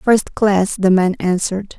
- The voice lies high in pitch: Yes, high, 200 Hz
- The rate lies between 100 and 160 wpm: Yes, slow, 135 wpm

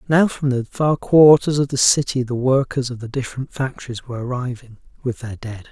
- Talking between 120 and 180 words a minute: No, average, 200 wpm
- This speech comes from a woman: No, male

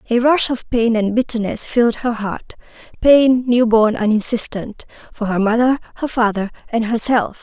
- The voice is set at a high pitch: Yes, high, 230 Hz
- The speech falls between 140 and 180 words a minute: Yes, average, 160 wpm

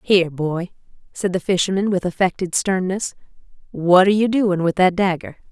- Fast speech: No, average, 165 wpm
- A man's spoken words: No, female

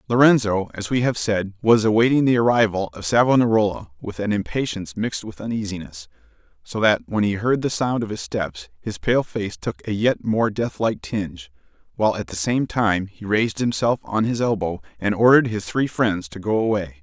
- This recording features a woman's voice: No, male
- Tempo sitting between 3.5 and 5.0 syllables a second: No, 5.4 syllables/s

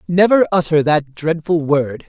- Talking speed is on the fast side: No, average, 145 wpm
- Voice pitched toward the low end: No, medium, 160 Hz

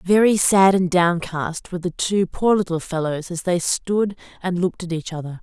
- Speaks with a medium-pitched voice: Yes, medium, 180 Hz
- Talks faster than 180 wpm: Yes, average, 200 wpm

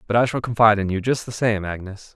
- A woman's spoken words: No, male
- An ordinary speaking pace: No, fast, 280 wpm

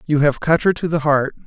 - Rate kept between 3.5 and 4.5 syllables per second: No, 5.7 syllables/s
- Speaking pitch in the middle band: Yes, medium, 150 Hz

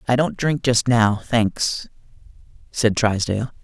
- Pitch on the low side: Yes, low, 115 Hz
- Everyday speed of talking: No, slow, 130 wpm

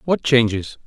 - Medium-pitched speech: No, low, 120 Hz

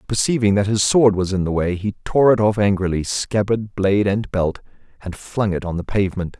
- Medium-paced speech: No, fast, 215 wpm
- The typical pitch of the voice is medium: No, low, 100 Hz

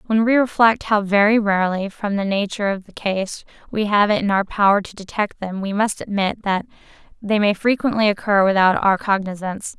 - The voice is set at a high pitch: Yes, high, 205 Hz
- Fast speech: No, average, 195 wpm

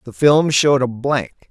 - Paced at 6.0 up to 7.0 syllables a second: No, 4.8 syllables/s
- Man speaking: Yes, male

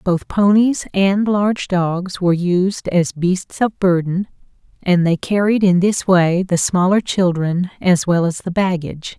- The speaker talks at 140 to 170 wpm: Yes, average, 165 wpm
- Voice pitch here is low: No, medium, 185 Hz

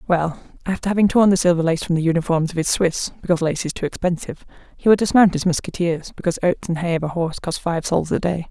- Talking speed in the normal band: No, fast, 245 wpm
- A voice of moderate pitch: Yes, medium, 170 Hz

